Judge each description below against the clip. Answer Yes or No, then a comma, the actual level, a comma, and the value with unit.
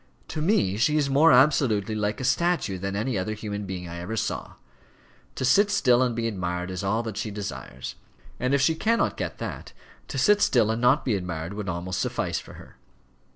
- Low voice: Yes, low, 110 Hz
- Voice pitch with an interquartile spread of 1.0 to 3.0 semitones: No, wide, 5.6 semitones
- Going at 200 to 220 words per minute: Yes, fast, 205 wpm